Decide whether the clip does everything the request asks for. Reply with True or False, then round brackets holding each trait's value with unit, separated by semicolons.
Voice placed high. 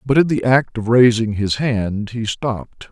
False (115 Hz)